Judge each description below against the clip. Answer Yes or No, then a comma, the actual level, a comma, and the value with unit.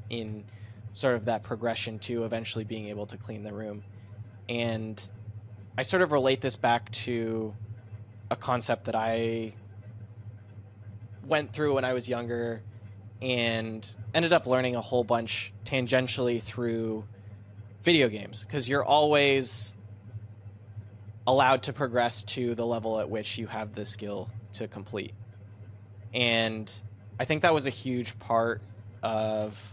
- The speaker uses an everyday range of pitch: No, narrow, 2.2 semitones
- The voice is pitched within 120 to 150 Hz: No, low, 110 Hz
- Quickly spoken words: No, slow, 135 wpm